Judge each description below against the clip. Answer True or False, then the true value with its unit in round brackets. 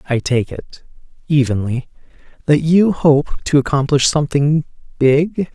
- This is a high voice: False (145 Hz)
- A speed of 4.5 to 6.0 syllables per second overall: False (4.3 syllables/s)